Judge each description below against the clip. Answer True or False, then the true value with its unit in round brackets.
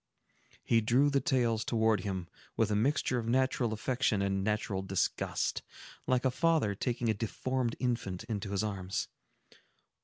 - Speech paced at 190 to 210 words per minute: False (150 wpm)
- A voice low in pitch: True (115 Hz)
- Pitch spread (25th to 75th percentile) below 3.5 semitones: False (3.8 semitones)